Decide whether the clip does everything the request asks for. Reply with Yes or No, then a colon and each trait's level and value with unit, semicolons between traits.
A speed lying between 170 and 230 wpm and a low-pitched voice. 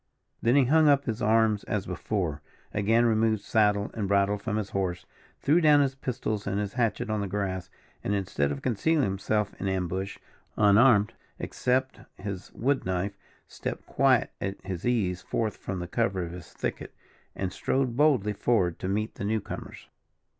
Yes: average, 175 wpm; low, 105 Hz